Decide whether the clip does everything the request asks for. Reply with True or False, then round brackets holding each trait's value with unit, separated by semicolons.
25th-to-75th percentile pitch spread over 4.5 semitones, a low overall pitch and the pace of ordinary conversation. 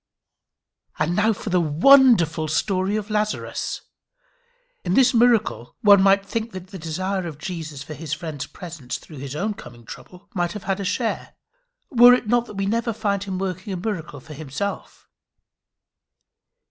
False (4.9 semitones; 190 Hz; 160 wpm)